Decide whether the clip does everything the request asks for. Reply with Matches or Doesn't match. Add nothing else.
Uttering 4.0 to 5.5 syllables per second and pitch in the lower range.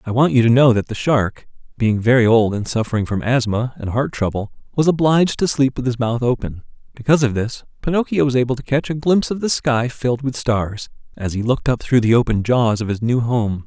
Doesn't match